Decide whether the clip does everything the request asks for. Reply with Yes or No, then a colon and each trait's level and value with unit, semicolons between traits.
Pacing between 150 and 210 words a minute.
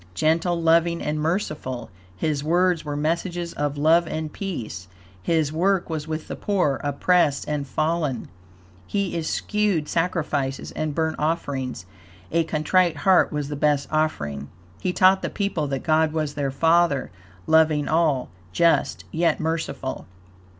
No: average, 140 wpm